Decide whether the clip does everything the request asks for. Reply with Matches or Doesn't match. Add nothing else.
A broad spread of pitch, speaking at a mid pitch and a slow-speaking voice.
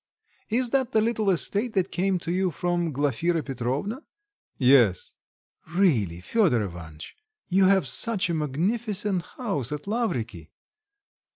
Matches